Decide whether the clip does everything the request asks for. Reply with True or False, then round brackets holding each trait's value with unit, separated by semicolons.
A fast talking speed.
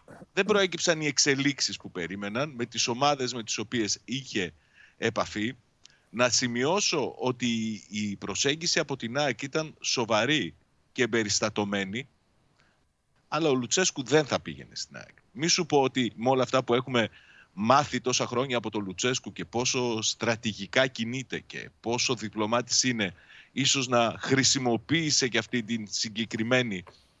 False (140 wpm)